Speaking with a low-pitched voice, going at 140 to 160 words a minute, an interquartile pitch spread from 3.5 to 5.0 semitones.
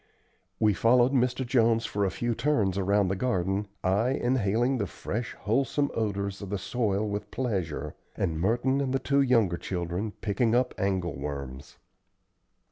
Yes: low, 105 Hz; average, 155 wpm; average, 4.3 semitones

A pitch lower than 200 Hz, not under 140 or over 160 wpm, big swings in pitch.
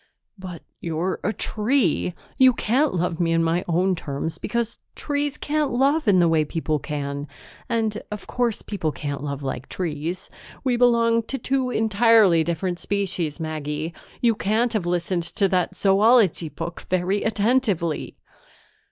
Yes: medium, 185 Hz; average, 150 wpm; wide, 5.8 semitones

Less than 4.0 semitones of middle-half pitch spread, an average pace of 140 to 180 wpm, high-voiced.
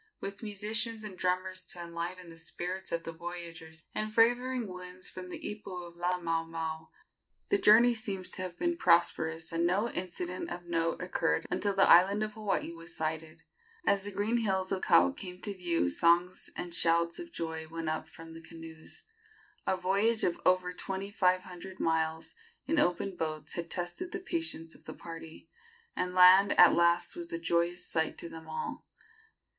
No: average, 3.0 semitones; average, 175 wpm; medium, 180 Hz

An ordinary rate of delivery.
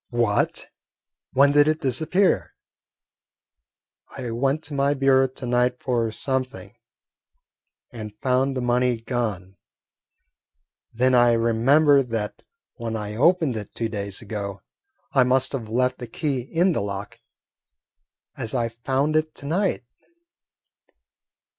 No: slow, 125 wpm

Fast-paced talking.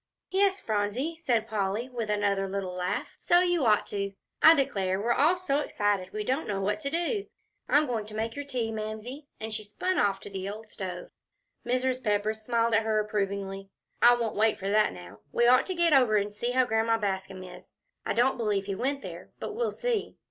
Yes: fast, 210 wpm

